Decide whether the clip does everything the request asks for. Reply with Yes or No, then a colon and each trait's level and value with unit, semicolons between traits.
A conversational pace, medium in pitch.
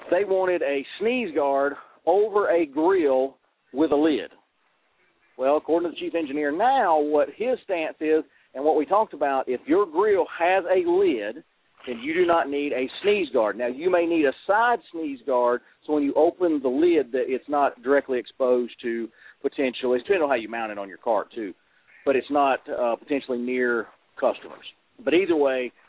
Yes: average, 190 wpm; medium, 150 Hz